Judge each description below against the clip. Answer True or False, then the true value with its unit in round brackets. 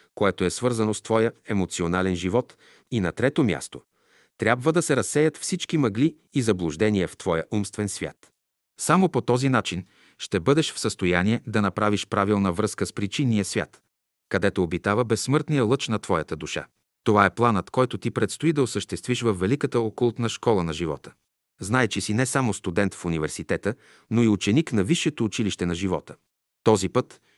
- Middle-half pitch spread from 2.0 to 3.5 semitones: False (4.2 semitones)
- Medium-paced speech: False (170 wpm)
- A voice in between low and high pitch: False (110 Hz)